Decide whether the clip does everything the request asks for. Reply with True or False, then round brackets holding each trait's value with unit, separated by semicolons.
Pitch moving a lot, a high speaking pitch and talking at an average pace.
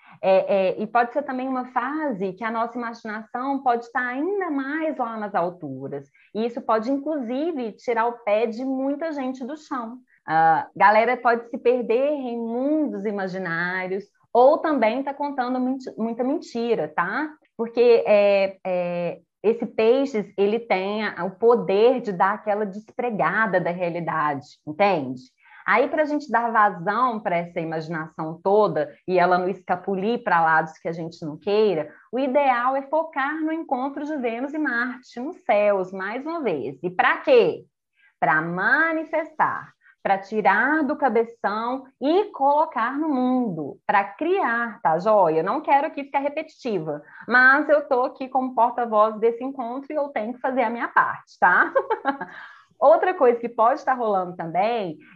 True (5.8 semitones; 235 Hz; 160 wpm)